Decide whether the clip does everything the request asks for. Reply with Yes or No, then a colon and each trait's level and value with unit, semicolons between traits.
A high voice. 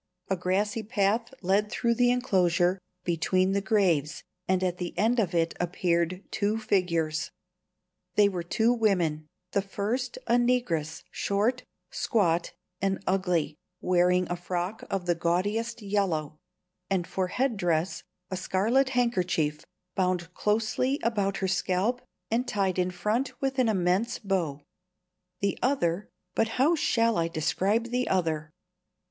Yes: high, 195 Hz